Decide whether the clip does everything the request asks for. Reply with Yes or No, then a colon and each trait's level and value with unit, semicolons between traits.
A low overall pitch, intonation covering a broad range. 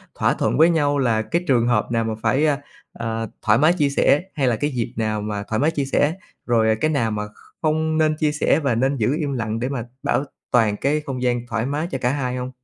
No: low, 125 Hz; average, 4.5 semitones